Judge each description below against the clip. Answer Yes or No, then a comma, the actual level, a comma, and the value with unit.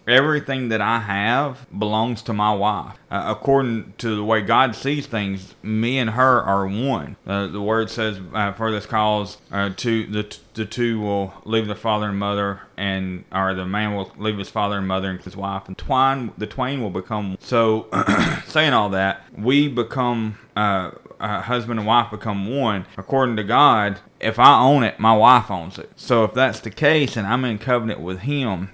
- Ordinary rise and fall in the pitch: Yes, average, 3.3 semitones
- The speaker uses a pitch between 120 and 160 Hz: No, low, 110 Hz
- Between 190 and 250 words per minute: Yes, average, 200 wpm